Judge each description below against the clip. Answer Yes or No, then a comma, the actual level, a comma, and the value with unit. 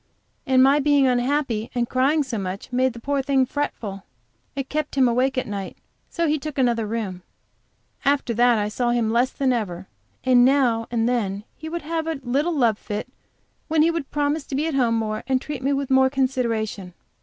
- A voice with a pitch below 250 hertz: No, very high, 255 Hz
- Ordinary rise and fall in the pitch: Yes, average, 3.7 semitones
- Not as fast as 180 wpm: No, average, 200 wpm